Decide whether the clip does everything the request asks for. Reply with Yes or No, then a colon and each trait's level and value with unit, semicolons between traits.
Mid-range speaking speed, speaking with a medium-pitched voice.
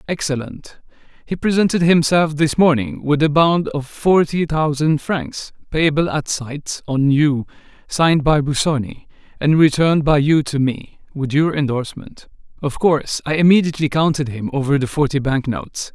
Yes: average, 150 wpm; medium, 150 Hz